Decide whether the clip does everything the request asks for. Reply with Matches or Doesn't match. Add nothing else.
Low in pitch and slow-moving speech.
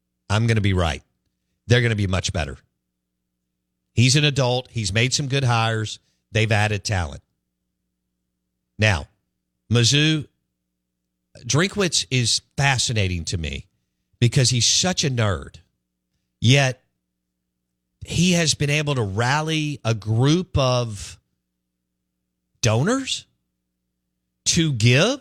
Matches